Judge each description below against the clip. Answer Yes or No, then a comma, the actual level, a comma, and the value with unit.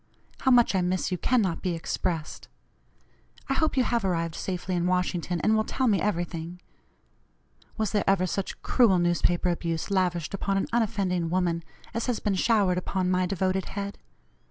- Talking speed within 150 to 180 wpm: Yes, average, 170 wpm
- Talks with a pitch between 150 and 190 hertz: Yes, medium, 185 Hz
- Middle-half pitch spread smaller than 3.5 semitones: Yes, average, 2.8 semitones